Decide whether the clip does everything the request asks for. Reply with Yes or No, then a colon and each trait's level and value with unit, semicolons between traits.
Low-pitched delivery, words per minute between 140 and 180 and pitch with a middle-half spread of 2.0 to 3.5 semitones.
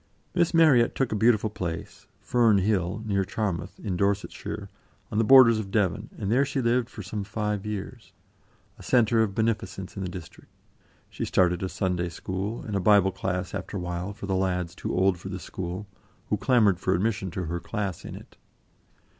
No: low, 100 Hz; average, 190 wpm; average, 3.1 semitones